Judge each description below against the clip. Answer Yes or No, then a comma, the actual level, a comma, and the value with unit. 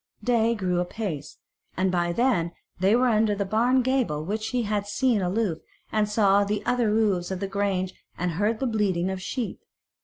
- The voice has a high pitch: Yes, high, 205 Hz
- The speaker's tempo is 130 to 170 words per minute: No, average, 185 wpm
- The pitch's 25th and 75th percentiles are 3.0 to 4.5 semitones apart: Yes, average, 3.6 semitones